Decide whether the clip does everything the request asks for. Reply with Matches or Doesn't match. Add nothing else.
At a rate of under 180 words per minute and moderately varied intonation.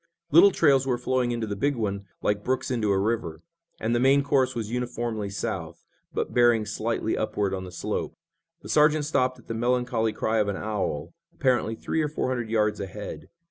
Doesn't match